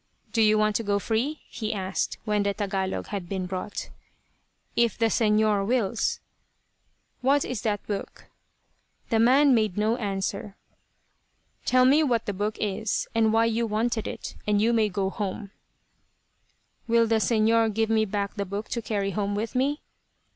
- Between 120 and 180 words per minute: Yes, average, 165 wpm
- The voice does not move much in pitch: Yes, narrow, 2.2 semitones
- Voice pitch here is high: Yes, high, 215 Hz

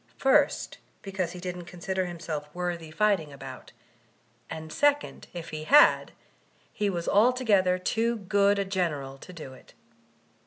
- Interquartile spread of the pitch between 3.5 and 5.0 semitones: Yes, average, 3.9 semitones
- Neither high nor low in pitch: Yes, medium, 180 Hz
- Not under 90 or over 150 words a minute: Yes, average, 145 wpm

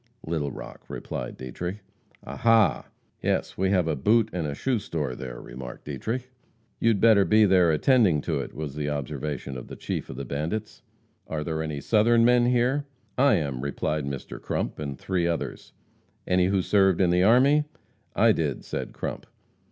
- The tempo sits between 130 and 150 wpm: No, average, 170 wpm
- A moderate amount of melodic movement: No, wide, 7.0 semitones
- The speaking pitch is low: Yes, very low, 90 Hz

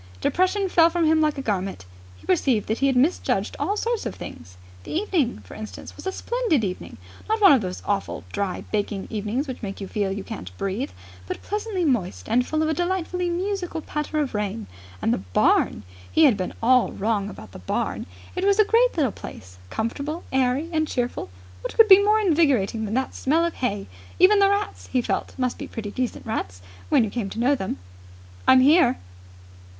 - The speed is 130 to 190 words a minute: No, fast, 205 wpm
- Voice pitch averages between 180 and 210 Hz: No, very high, 260 Hz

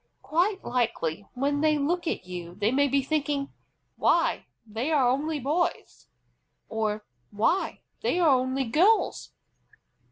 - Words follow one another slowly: Yes, slow, 130 wpm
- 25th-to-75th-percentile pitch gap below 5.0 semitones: No, wide, 5.4 semitones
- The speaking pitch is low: No, very high, 275 Hz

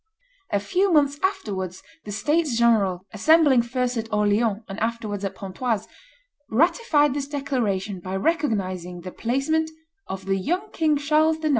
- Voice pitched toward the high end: Yes, high, 235 Hz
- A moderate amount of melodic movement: No, wide, 7.1 semitones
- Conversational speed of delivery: Yes, average, 145 wpm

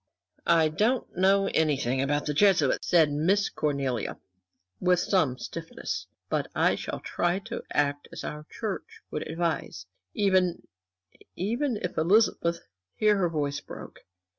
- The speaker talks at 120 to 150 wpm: Yes, slow, 135 wpm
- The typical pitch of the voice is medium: Yes, medium, 170 Hz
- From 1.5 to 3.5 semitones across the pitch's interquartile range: No, average, 4.9 semitones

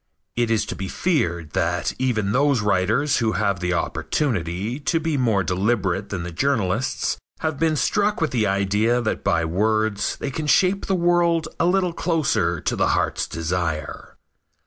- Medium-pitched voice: No, low, 115 Hz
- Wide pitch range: Yes, wide, 8.2 semitones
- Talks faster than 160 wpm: Yes, average, 170 wpm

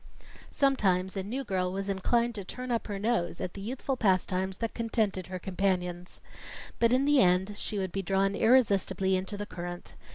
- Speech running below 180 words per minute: No, average, 185 wpm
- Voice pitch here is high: Yes, high, 195 Hz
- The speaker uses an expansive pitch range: No, average, 3.8 semitones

